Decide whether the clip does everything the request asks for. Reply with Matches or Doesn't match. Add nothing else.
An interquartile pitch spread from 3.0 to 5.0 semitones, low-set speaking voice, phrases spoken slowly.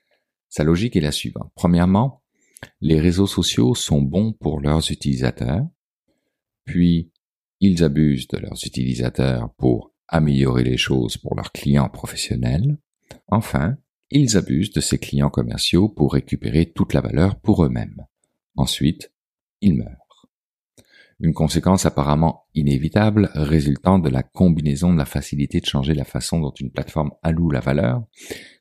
Matches